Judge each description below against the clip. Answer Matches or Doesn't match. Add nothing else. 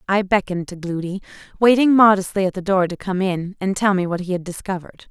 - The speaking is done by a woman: Matches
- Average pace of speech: Doesn't match